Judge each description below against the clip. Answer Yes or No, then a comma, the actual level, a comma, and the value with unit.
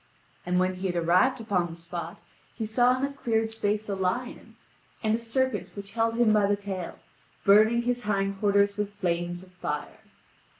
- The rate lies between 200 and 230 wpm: No, average, 185 wpm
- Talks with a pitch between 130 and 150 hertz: No, high, 205 Hz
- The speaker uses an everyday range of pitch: Yes, average, 3.7 semitones